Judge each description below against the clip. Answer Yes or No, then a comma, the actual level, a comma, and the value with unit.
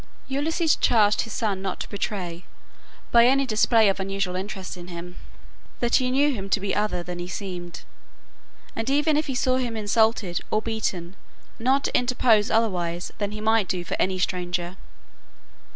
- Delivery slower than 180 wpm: Yes, average, 170 wpm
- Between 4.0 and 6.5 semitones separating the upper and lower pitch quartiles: Yes, average, 4.6 semitones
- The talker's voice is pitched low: No, high, 210 Hz